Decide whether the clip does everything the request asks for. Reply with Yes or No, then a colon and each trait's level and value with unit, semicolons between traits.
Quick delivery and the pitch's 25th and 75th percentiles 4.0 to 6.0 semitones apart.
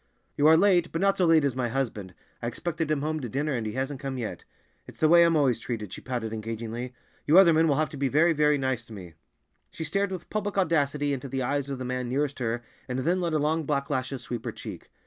Yes: fast, 260 wpm; average, 4.3 semitones